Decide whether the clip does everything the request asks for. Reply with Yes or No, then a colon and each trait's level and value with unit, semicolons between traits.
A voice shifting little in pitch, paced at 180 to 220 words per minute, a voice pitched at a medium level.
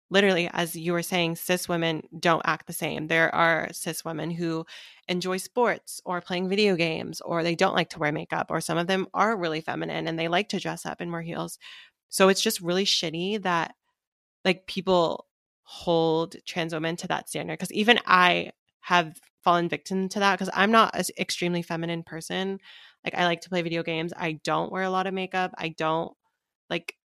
Yes: narrow, 2.2 semitones; average, 200 wpm; medium, 175 Hz